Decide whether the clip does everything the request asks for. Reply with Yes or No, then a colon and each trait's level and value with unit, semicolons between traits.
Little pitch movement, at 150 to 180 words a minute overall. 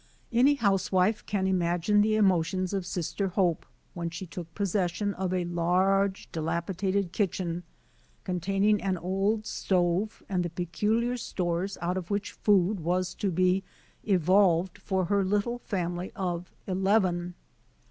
No: narrow, 2.3 semitones; slow, 135 wpm